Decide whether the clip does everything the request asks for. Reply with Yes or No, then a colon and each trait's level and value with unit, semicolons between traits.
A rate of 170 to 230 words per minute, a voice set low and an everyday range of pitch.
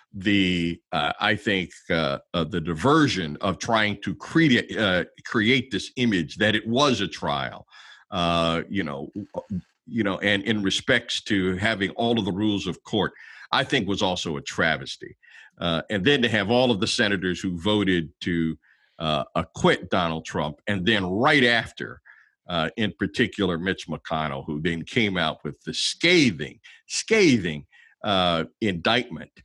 No: average, 160 wpm; low, 100 Hz; average, 4.1 semitones